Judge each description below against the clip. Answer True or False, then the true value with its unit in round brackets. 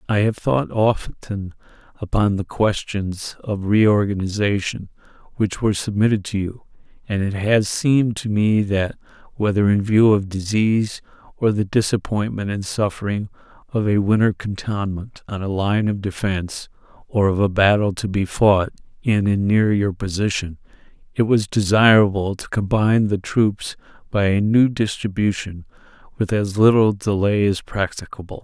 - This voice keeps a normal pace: True (145 wpm)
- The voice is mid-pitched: False (105 Hz)